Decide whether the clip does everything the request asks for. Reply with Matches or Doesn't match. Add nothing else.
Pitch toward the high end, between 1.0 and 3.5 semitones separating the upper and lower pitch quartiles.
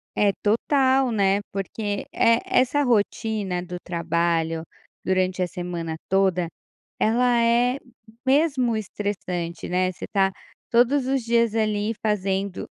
Doesn't match